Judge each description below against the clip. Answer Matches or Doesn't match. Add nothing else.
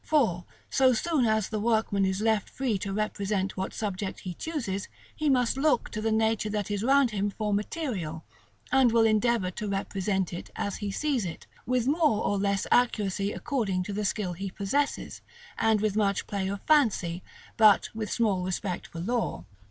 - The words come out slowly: Doesn't match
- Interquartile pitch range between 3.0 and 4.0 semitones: Matches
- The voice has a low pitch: Doesn't match